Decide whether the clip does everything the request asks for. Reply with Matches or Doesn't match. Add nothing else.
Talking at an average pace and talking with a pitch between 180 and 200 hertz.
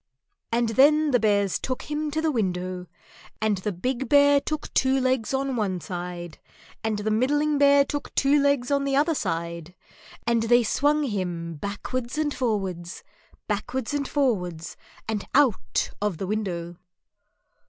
Doesn't match